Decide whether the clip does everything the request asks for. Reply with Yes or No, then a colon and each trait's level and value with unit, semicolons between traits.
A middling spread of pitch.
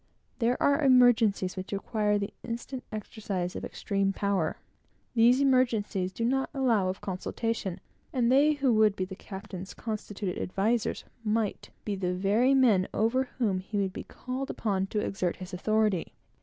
Yes: average, 3.9 semitones